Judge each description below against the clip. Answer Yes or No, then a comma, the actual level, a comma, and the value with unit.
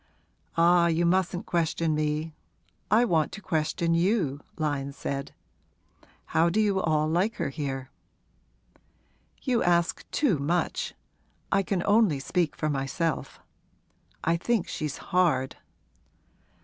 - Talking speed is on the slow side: Yes, slow, 120 wpm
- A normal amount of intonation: Yes, average, 3.3 semitones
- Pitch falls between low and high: Yes, medium, 165 Hz